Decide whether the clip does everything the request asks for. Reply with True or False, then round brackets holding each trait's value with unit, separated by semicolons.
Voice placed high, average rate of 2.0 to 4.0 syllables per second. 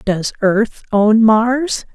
True (220 Hz; 2.5 syllables/s)